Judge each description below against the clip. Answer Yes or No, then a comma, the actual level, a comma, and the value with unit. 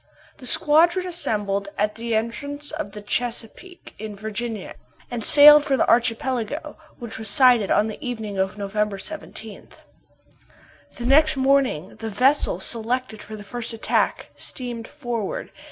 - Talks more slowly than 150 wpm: Yes, average, 140 wpm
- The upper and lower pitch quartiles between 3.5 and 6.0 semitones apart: Yes, average, 4.5 semitones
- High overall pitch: Yes, high, 235 Hz